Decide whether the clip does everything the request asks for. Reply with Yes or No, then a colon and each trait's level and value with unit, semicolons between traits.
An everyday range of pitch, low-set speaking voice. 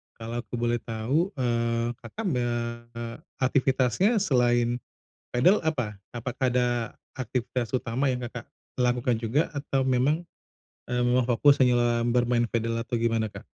No: narrow, 1.6 semitones; low, 120 Hz